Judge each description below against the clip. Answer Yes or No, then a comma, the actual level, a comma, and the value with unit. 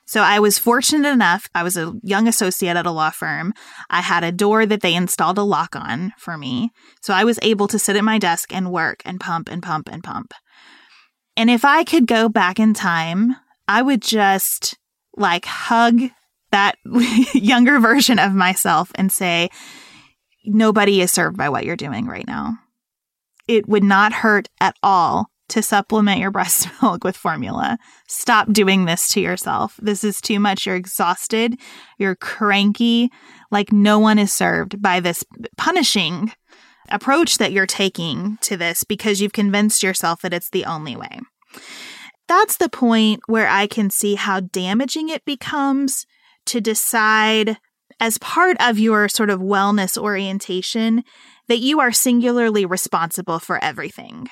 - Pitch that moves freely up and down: No, average, 3.8 semitones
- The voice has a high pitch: Yes, high, 210 Hz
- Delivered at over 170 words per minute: No, average, 165 wpm